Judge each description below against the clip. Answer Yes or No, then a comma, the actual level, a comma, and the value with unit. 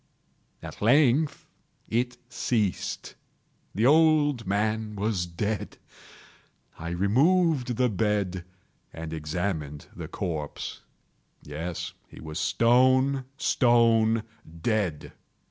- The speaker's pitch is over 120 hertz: No, low, 110 Hz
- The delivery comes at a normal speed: No, slow, 90 wpm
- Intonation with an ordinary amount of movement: No, wide, 5.9 semitones